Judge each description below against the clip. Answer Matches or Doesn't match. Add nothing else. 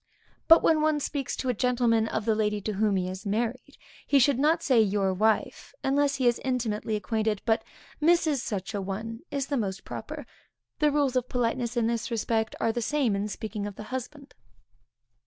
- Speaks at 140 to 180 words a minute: Doesn't match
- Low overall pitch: Doesn't match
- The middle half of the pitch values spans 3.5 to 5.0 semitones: Matches